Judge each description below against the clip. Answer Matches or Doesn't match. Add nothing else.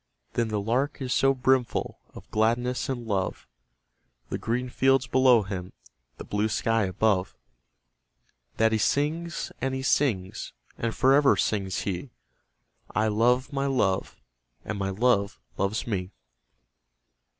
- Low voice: Matches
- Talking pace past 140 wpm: Doesn't match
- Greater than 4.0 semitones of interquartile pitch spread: Matches